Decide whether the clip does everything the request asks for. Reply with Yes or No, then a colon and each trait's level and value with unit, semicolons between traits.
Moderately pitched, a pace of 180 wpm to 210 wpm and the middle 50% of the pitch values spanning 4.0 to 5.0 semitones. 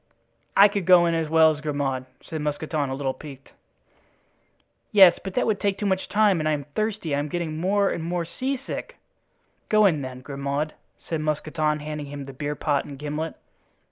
Yes: medium, 155 Hz; average, 195 wpm; average, 4.5 semitones